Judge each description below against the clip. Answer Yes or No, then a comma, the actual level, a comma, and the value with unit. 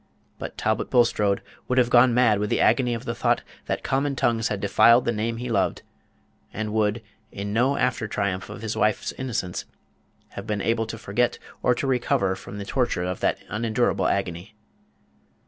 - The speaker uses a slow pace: No, average, 180 wpm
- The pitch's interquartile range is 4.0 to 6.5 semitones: No, average, 3.1 semitones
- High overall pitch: No, low, 110 Hz